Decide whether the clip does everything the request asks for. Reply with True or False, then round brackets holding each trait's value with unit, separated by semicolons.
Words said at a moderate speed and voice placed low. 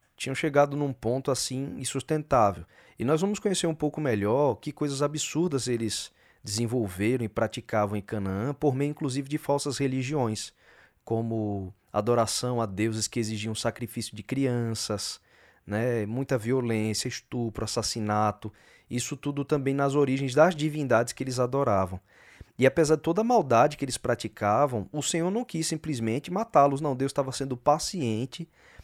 True (150 wpm; 130 Hz)